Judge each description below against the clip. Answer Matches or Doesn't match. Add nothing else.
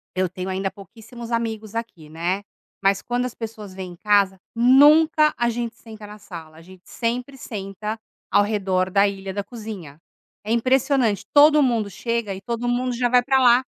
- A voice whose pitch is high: Matches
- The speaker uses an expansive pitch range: Doesn't match